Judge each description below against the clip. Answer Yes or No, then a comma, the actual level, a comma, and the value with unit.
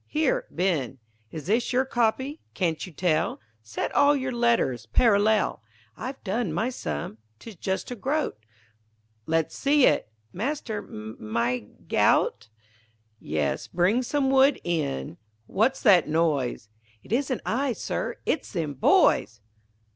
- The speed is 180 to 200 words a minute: No, slow, 135 wpm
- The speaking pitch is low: No, high, 200 Hz